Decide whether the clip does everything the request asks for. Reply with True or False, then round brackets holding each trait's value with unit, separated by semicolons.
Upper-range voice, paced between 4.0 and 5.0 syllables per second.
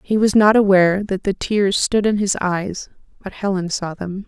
True (195 Hz; 4.8 syllables/s)